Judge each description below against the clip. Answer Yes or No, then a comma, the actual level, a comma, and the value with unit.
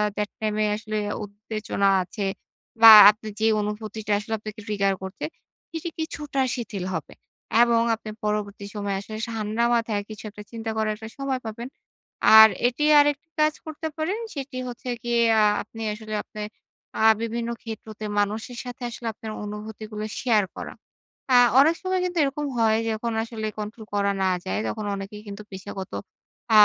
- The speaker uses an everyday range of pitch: No, narrow, 2.3 semitones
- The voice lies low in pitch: No, high, 220 Hz